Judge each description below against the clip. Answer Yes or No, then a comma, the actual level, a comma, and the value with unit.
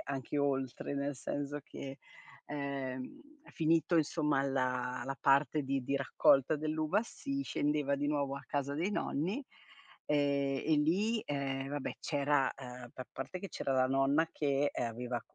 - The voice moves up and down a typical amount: No, narrow, 2.0 semitones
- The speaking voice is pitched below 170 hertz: Yes, medium, 140 Hz